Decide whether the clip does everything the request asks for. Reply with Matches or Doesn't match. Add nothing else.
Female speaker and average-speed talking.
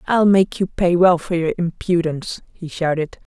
Matches